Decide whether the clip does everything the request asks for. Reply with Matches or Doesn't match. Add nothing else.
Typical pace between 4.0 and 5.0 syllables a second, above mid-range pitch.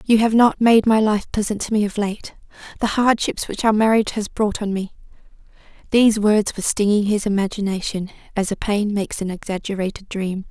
Doesn't match